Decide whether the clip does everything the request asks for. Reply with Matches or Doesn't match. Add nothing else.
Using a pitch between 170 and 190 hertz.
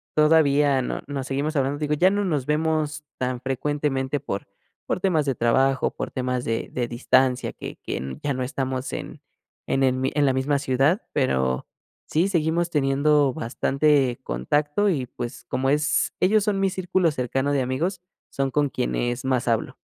Doesn't match